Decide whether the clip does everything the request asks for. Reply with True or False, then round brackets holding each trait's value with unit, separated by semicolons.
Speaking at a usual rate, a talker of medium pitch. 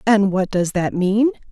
False (195 wpm; 200 Hz)